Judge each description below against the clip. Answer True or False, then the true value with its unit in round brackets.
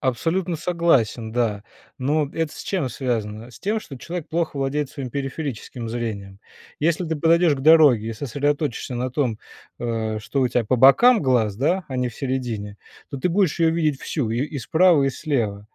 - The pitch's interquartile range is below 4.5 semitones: False (5.4 semitones)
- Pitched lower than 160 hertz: True (135 Hz)